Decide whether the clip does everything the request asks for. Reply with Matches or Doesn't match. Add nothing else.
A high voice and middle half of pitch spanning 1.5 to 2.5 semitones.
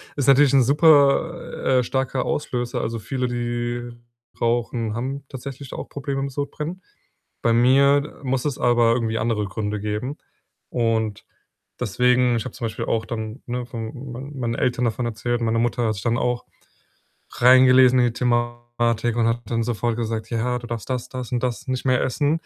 Doesn't match